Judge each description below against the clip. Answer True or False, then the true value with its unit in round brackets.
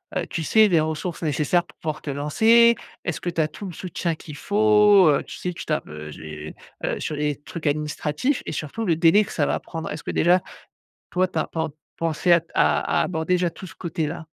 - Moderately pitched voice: True (165 Hz)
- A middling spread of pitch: True (3.3 semitones)